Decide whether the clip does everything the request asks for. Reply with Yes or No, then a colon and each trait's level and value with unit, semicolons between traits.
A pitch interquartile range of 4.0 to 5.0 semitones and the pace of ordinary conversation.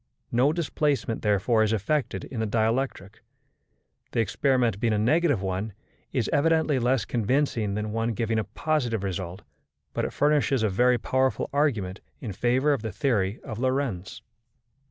Yes: average, 4.4 semitones; average, 155 wpm